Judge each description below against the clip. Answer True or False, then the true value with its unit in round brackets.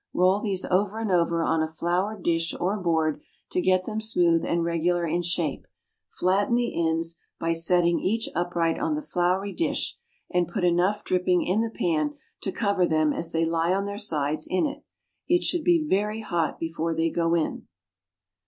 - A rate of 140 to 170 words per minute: False (185 wpm)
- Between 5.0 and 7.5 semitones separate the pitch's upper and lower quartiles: False (3.4 semitones)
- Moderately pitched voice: True (175 Hz)